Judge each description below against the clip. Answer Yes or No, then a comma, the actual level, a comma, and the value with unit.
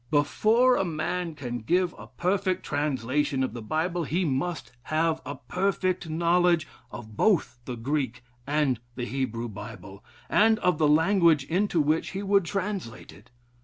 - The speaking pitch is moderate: Yes, medium, 155 Hz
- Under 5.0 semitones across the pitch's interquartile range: No, wide, 5.5 semitones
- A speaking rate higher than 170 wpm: No, average, 150 wpm